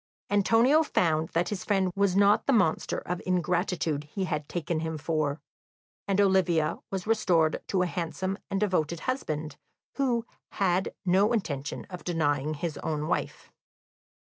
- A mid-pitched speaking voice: Yes, medium, 180 Hz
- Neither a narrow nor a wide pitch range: Yes, average, 3.9 semitones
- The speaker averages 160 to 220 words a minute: No, average, 145 wpm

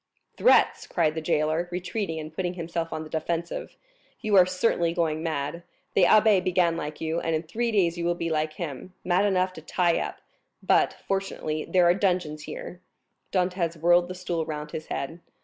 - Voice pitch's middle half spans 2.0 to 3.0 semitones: Yes, narrow, 2.5 semitones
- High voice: No, medium, 170 Hz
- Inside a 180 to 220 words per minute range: Yes, average, 185 wpm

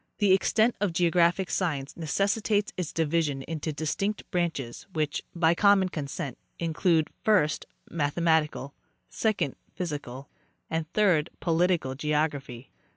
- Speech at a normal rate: No, slow, 110 wpm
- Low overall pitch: No, medium, 165 Hz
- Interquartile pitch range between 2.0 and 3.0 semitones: No, average, 3.7 semitones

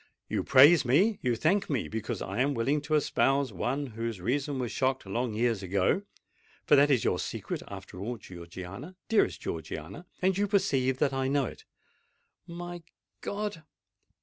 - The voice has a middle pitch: No, low, 130 Hz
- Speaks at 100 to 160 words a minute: Yes, average, 150 wpm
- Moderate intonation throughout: No, wide, 5.9 semitones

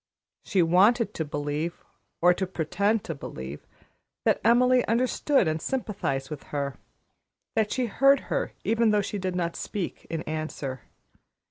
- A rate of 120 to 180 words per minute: Yes, average, 145 wpm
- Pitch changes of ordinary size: No, wide, 6.5 semitones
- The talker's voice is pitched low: No, medium, 185 Hz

